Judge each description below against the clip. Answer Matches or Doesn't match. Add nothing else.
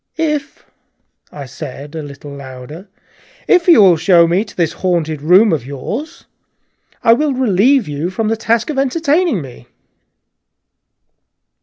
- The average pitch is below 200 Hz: Matches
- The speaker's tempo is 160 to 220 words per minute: Doesn't match